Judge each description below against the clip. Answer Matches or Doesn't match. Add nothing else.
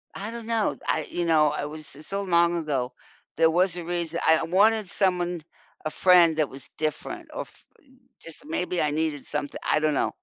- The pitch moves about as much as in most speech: Matches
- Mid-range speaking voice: Matches